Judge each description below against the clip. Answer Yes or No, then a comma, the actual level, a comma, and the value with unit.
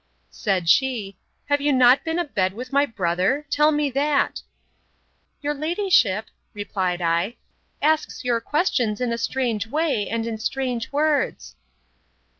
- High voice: Yes, very high, 250 Hz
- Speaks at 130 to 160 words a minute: Yes, average, 140 wpm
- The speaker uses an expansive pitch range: Yes, wide, 5.8 semitones